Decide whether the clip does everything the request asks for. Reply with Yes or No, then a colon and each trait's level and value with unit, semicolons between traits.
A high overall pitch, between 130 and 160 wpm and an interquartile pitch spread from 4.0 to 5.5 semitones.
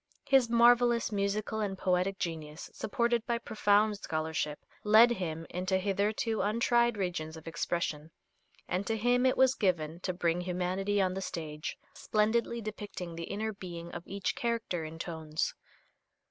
Yes: high, 195 Hz; average, 145 wpm; average, 4.5 semitones